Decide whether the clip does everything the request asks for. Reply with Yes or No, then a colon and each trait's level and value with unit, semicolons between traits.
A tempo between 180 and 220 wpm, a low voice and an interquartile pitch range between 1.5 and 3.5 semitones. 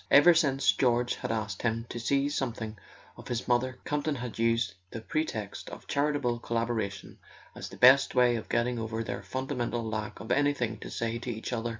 Yes: average, 195 wpm; low, 120 Hz; average, 2.8 semitones